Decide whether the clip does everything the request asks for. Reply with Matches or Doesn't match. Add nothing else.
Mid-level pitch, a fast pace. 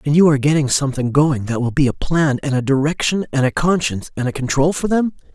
Matches